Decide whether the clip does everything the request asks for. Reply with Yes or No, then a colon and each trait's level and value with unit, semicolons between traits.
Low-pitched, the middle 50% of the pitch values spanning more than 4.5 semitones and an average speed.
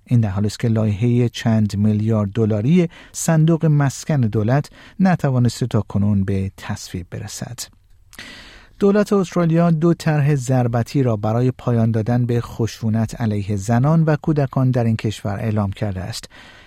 Yes: low, 115 Hz; average, 5.2 semitones; average, 135 wpm